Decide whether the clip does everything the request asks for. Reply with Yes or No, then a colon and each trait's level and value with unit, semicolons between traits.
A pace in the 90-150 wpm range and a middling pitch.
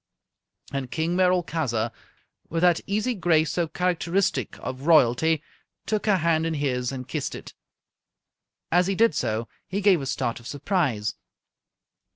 Yes: average, 145 wpm; medium, 160 Hz